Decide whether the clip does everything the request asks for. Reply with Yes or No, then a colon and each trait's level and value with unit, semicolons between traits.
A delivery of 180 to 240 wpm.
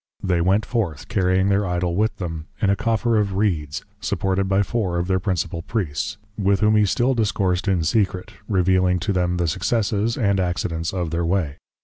Yes: average, 190 wpm